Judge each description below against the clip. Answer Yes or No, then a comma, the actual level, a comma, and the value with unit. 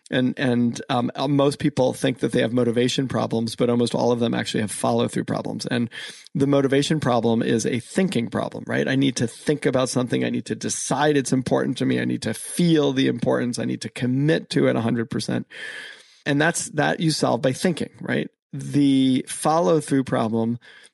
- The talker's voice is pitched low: Yes, low, 130 Hz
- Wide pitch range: No, average, 3.3 semitones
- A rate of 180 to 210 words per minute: Yes, average, 200 wpm